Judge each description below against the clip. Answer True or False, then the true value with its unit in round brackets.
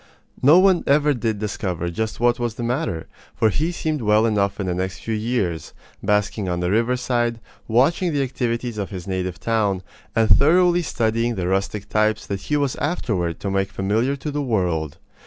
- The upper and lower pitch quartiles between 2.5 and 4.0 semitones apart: False (4.8 semitones)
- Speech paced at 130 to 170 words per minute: False (185 wpm)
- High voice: False (110 Hz)